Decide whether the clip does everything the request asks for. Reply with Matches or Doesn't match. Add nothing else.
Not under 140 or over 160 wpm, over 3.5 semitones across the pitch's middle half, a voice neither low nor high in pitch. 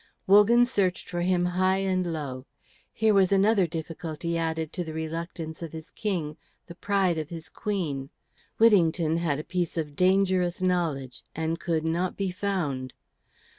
Doesn't match